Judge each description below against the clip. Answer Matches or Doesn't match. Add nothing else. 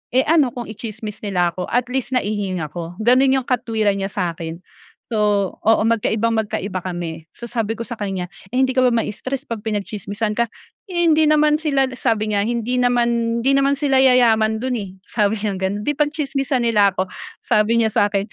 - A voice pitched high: Matches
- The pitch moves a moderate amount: Matches